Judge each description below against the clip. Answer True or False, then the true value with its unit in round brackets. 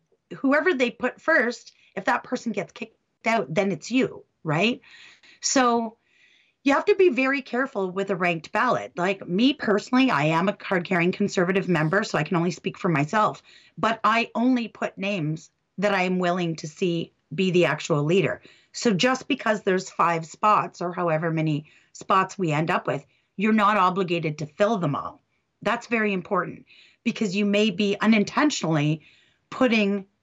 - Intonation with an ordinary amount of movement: True (4.8 semitones)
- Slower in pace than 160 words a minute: False (175 wpm)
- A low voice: False (200 Hz)